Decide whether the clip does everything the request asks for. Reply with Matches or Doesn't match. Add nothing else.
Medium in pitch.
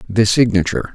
Doesn't match